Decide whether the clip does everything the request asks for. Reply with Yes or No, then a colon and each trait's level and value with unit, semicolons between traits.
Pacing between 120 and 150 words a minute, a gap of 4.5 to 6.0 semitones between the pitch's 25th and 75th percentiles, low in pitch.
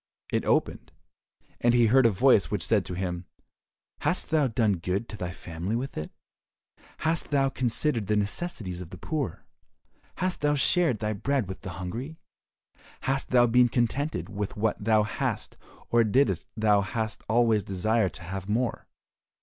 No: average, 160 wpm; average, 5.1 semitones; low, 110 Hz